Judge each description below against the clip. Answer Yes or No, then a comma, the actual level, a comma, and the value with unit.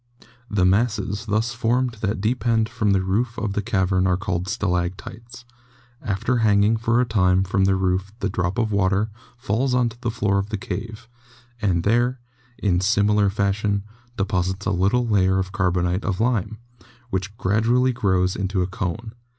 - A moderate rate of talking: Yes, average, 165 wpm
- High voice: No, low, 100 Hz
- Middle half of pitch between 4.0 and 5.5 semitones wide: No, average, 3.2 semitones